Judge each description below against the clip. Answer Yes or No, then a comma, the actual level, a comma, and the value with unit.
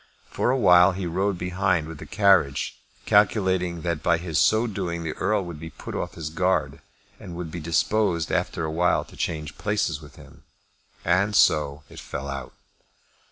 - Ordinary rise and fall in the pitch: Yes, average, 3.4 semitones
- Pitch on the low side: Yes, very low, 85 Hz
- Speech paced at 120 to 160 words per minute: No, average, 170 wpm